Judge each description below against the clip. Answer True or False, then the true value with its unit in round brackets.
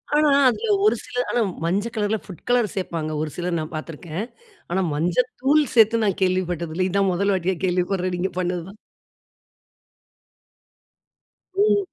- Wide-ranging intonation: False (3.8 semitones)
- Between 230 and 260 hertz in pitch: False (185 Hz)